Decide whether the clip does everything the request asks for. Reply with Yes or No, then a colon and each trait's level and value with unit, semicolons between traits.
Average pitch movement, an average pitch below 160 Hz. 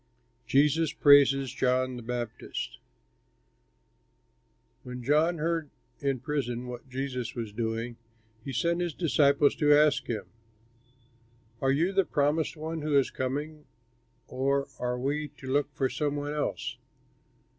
Yes: average, 3.0 semitones; medium, 140 Hz